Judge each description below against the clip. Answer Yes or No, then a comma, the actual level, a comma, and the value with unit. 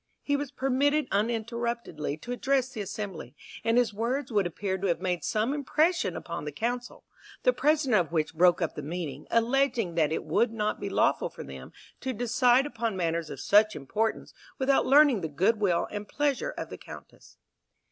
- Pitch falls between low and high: No, high, 220 Hz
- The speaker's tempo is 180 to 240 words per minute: Yes, average, 185 wpm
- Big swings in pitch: Yes, wide, 6.8 semitones